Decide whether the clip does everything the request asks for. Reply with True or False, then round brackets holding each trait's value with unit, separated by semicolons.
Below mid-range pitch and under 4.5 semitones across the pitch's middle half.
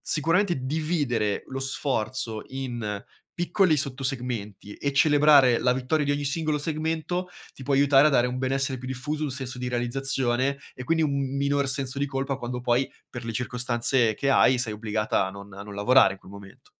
True (130 Hz; 2.9 semitones)